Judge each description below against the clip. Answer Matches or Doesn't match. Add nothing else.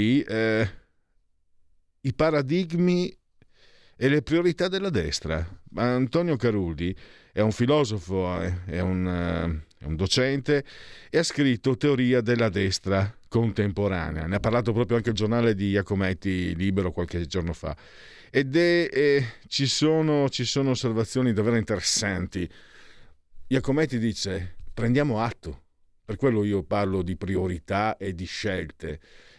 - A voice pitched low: Matches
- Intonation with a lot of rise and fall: Matches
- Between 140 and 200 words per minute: Doesn't match